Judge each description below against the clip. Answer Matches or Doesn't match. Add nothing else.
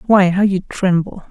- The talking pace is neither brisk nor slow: Matches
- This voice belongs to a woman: Matches